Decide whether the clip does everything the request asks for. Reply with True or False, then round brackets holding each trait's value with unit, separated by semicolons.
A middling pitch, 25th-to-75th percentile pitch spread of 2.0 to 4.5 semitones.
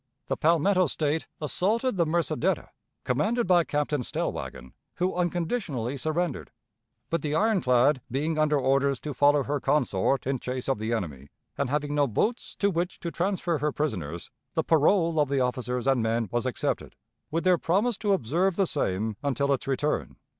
False (145 Hz; 5.2 semitones)